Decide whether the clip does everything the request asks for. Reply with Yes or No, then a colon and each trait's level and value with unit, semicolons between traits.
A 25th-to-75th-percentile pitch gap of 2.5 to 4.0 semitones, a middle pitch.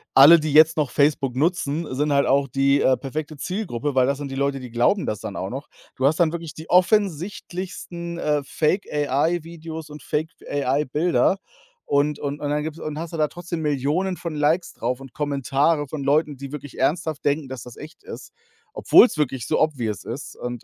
Yes: average, 2.9 semitones; medium, 150 Hz